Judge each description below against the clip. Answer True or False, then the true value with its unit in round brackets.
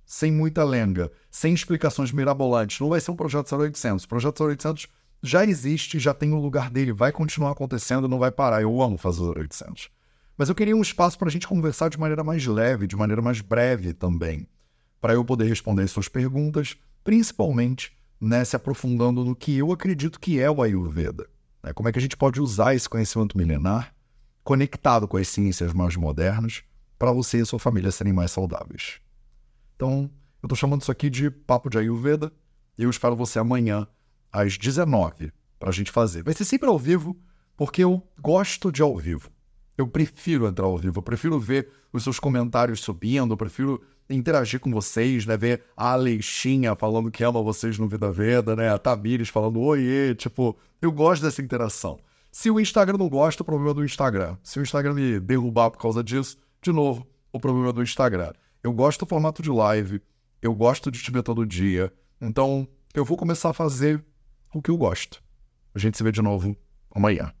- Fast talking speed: True (195 wpm)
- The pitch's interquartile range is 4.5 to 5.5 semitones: True (5.1 semitones)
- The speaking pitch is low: True (125 Hz)